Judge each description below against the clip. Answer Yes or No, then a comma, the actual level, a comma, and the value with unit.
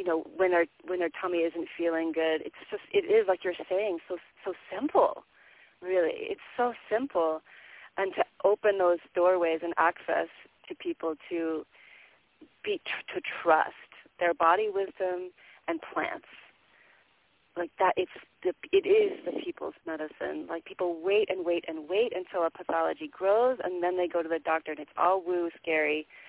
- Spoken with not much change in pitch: No, average, 4.3 semitones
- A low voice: No, medium, 180 Hz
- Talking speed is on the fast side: No, average, 170 wpm